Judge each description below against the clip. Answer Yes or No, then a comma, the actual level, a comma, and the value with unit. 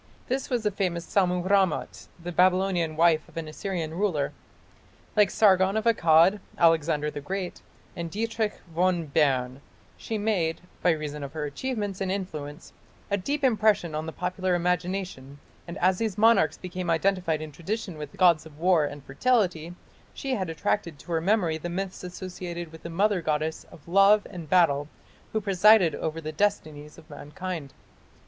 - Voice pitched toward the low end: No, medium, 175 Hz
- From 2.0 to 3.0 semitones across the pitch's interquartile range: No, average, 3.8 semitones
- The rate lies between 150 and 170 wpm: Yes, average, 165 wpm